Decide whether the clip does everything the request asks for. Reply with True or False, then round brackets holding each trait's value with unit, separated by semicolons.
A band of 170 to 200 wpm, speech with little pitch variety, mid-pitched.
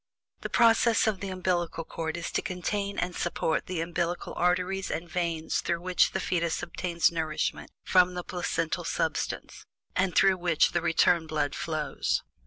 False (160 wpm; 1.8 semitones; 175 Hz)